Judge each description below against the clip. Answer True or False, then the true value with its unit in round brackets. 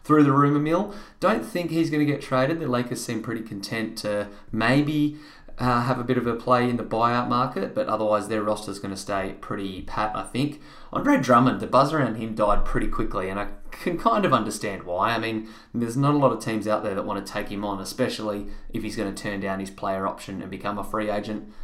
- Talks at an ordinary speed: False (245 wpm)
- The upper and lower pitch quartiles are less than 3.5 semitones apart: False (3.8 semitones)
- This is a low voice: True (110 Hz)